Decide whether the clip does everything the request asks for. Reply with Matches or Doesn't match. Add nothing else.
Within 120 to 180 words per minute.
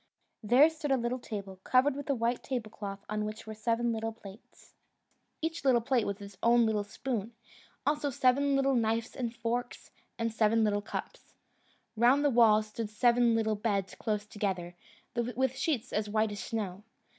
Matches